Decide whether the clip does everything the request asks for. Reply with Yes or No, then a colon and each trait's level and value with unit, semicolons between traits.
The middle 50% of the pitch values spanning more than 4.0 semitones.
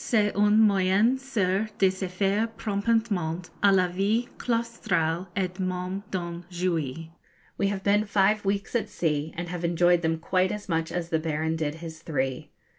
No: average, 3.6 semitones